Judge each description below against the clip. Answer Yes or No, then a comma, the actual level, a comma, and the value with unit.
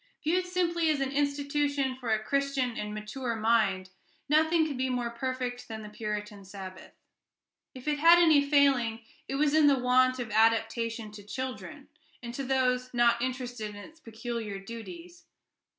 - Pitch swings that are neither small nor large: Yes, average, 4.1 semitones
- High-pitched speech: Yes, very high, 250 Hz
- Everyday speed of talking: Yes, average, 165 wpm